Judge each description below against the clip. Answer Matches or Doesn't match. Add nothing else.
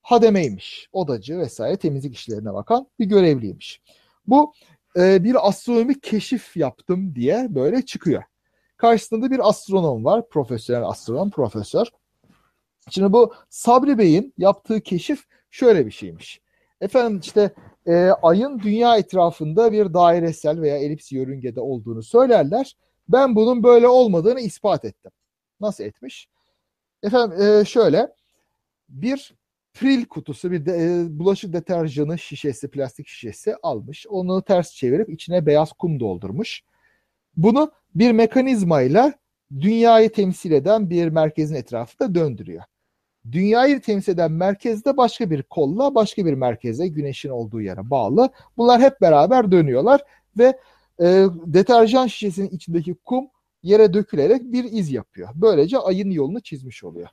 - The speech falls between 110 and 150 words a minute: Matches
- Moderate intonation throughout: Doesn't match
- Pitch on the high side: Matches